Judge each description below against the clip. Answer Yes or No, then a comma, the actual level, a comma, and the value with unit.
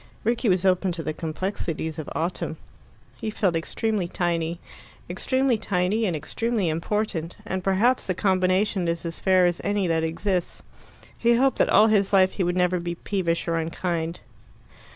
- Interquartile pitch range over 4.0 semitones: No, average, 3.6 semitones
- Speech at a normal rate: Yes, average, 165 wpm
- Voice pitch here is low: No, medium, 185 Hz